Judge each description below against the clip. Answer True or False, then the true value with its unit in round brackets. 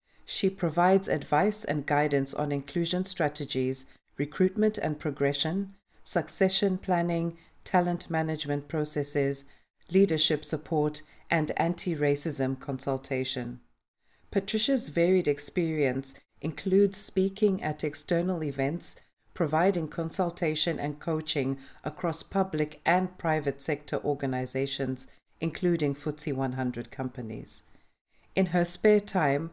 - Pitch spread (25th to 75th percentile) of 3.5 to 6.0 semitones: True (4.1 semitones)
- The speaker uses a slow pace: True (100 wpm)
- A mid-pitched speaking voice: True (155 Hz)